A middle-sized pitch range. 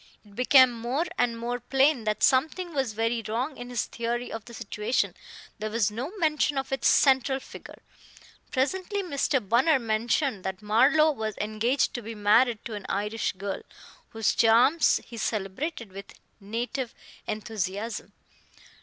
Yes: average, 3.8 semitones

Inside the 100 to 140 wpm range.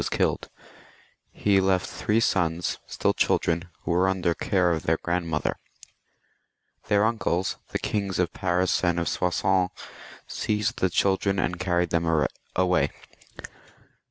Yes: slow, 135 wpm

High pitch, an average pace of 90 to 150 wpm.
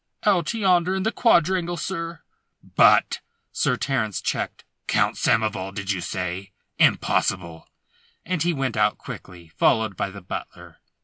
No: low, 110 Hz; average, 140 wpm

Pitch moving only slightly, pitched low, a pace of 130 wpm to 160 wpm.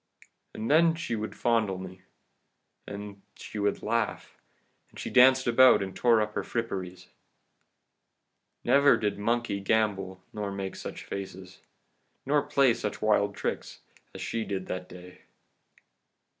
No: average, 3.7 semitones; low, 105 Hz; average, 140 wpm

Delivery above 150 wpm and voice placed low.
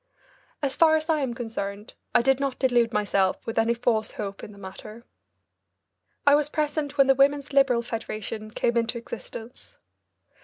No: average, 165 wpm; high, 235 Hz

